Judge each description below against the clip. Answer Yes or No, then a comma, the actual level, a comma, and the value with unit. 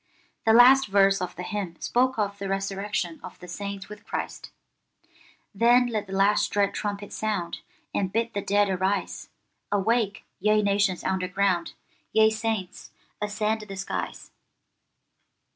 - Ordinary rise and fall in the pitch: No, narrow, 1.9 semitones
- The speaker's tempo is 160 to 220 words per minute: No, average, 140 wpm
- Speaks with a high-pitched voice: Yes, high, 205 Hz